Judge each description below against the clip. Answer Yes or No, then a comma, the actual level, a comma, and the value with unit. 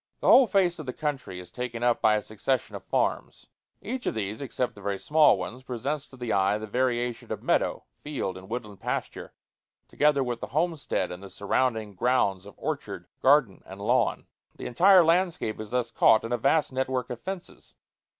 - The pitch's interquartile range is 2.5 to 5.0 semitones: No, wide, 5.6 semitones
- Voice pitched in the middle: No, low, 125 Hz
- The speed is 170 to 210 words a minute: Yes, average, 200 wpm